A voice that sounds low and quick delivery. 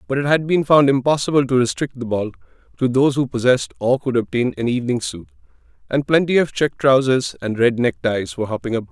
Yes: low, 130 Hz; fast, 210 wpm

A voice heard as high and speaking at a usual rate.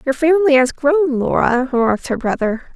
Yes: very high, 275 Hz; average, 175 wpm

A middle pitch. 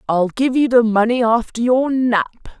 No: high, 235 Hz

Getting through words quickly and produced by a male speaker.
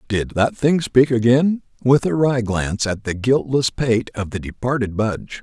No: average, 190 wpm; male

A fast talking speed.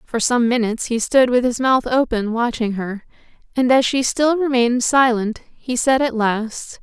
No: average, 185 wpm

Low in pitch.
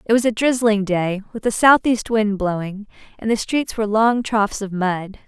No: high, 215 Hz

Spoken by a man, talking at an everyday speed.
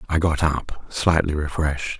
Yes: male; average, 150 wpm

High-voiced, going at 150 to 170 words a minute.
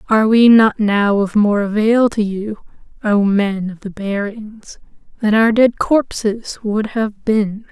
Yes: high, 215 Hz; average, 165 wpm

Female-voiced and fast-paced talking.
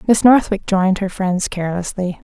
No: female; average, 155 wpm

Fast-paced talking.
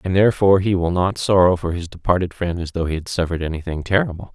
Yes: fast, 235 wpm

